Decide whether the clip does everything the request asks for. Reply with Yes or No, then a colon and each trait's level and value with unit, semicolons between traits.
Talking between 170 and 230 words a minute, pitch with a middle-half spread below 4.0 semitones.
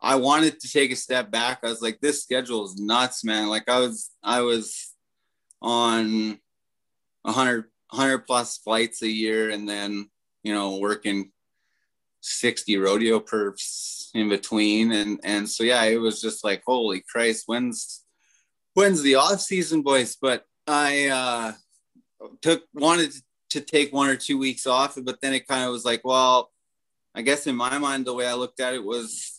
Yes: average, 175 wpm; average, 3.4 semitones